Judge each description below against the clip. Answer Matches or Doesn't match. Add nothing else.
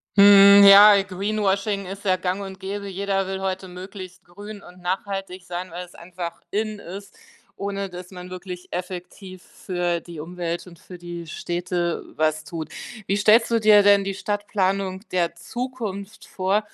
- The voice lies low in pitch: Doesn't match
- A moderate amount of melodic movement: Doesn't match